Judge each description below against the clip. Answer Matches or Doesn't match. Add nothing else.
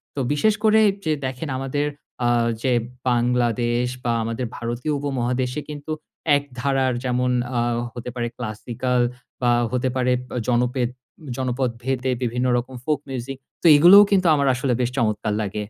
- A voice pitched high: Doesn't match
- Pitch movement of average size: Doesn't match